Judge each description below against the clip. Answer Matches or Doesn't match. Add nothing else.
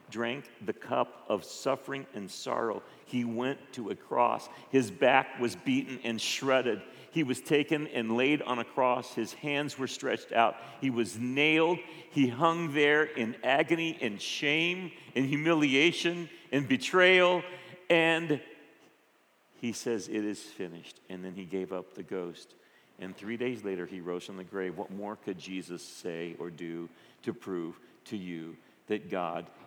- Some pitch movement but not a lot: Doesn't match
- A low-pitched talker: Matches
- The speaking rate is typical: Matches